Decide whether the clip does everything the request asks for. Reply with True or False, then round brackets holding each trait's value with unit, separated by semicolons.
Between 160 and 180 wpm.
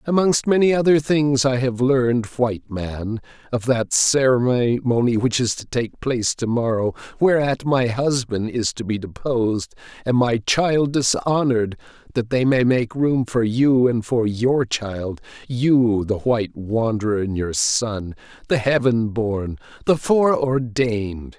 False (150 wpm)